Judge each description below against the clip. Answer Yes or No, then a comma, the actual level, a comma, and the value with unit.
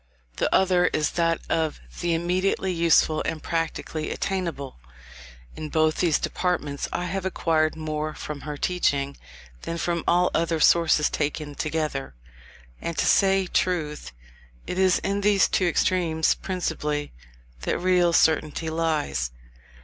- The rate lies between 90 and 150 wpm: Yes, slow, 135 wpm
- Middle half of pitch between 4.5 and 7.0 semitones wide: No, average, 2.7 semitones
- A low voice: No, medium, 165 Hz